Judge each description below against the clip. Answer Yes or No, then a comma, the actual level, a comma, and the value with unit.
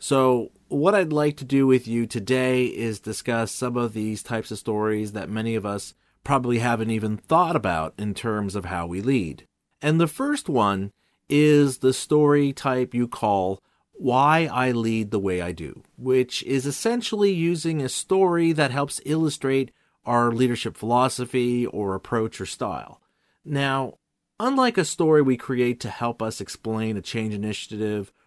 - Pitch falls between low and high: No, low, 120 Hz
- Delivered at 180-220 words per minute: No, average, 165 wpm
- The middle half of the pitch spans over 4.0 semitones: Yes, average, 4.6 semitones